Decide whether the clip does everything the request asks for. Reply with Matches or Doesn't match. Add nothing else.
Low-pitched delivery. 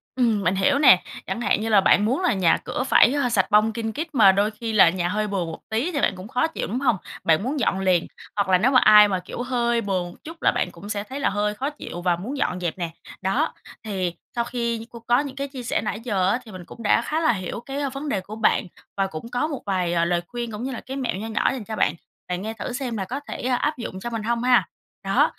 Doesn't match